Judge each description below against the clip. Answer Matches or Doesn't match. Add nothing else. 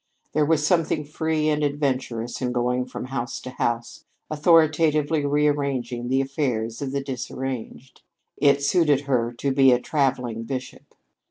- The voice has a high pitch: Doesn't match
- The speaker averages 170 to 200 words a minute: Doesn't match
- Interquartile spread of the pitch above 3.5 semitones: Doesn't match